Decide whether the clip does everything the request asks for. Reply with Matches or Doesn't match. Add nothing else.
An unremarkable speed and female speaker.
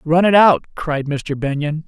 Doesn't match